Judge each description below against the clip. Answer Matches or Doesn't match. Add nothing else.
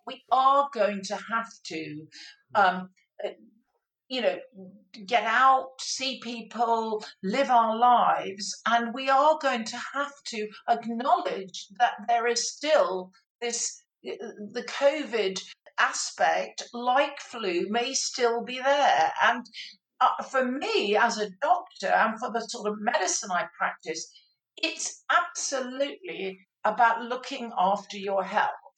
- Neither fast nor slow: Doesn't match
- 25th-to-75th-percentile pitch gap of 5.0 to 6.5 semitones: Doesn't match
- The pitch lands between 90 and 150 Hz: Doesn't match